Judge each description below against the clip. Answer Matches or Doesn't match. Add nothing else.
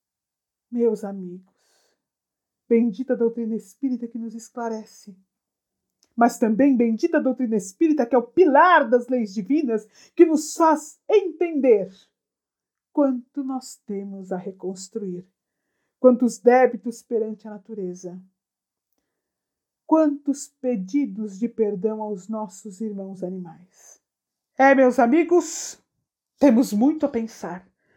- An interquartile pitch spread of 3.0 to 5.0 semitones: Matches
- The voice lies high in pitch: Matches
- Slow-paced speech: Matches